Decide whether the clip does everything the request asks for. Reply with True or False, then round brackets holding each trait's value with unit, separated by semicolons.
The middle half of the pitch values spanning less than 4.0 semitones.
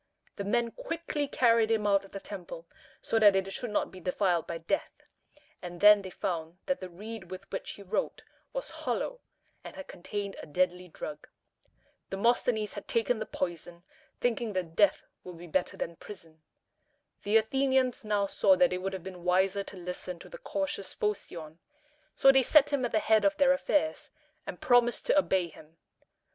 False (5.1 semitones)